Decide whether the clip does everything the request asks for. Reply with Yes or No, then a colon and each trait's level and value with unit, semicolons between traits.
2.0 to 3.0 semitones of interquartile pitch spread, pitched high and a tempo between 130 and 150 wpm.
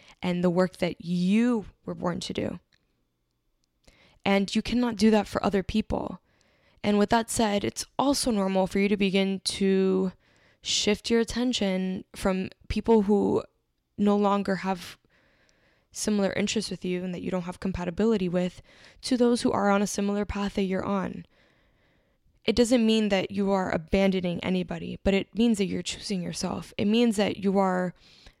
No: narrow, 2.5 semitones; high, 195 Hz; average, 170 wpm